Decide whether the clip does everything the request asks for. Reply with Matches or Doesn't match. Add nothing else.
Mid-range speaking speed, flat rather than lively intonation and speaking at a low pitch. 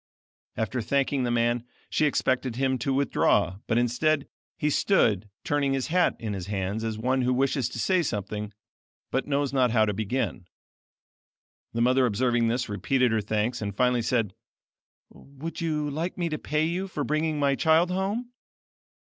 Doesn't match